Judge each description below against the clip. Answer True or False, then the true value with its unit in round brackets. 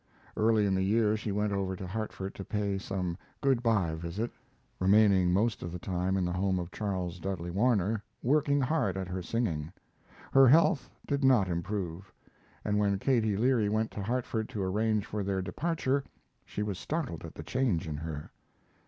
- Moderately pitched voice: False (100 Hz)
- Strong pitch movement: False (3.6 semitones)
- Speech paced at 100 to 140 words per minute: False (180 wpm)